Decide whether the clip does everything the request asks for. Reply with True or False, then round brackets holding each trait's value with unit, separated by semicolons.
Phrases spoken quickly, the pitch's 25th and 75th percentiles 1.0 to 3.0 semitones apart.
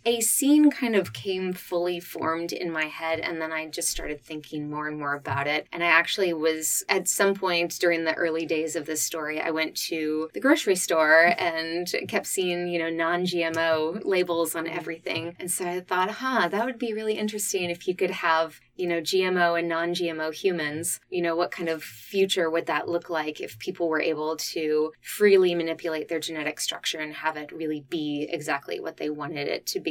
True (210 wpm; 2.4 semitones)